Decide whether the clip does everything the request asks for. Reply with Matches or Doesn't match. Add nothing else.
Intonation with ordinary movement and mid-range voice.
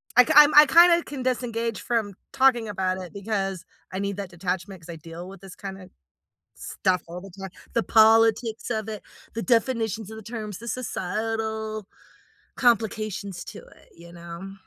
Doesn't match